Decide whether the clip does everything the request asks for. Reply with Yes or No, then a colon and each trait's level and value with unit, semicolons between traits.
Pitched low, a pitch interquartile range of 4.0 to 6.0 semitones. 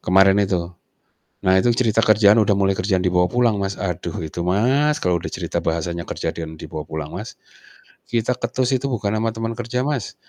Yes: low, 100 Hz; average, 4.7 semitones